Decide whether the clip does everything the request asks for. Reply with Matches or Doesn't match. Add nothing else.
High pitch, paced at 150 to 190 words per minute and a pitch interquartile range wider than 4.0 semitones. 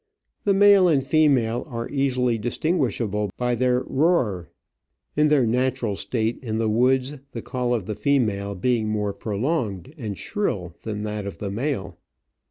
Doesn't match